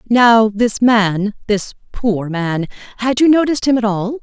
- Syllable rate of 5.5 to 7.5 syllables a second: No, 4.1 syllables/s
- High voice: Yes, high, 220 Hz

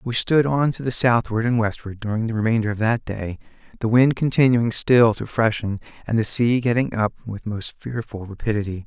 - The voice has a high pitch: No, low, 115 Hz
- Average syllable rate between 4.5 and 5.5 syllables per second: Yes, 5.2 syllables/s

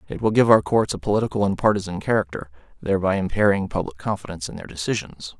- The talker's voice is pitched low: Yes, very low, 95 Hz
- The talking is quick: No, average, 190 wpm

